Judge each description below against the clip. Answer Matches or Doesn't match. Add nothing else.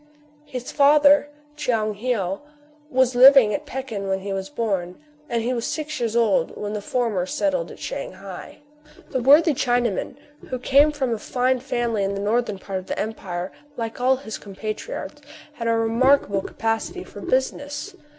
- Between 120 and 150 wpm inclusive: Doesn't match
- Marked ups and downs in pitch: Doesn't match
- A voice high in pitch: Matches